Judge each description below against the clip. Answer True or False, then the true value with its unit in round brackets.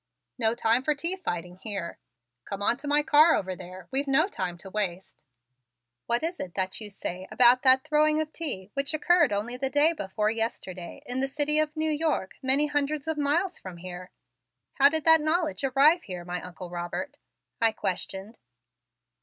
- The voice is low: False (260 Hz)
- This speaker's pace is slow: False (185 wpm)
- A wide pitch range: True (8.0 semitones)